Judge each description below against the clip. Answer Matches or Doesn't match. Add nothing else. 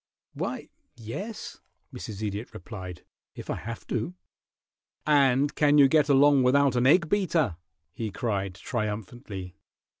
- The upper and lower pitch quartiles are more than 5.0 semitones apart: Matches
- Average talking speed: Doesn't match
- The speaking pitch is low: Matches